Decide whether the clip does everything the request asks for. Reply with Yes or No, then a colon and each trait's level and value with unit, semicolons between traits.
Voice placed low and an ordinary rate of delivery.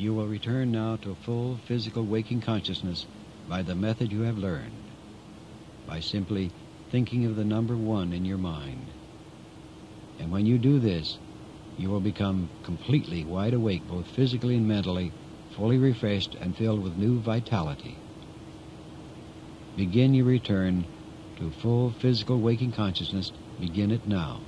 Yes: low, 105 Hz; average, 145 wpm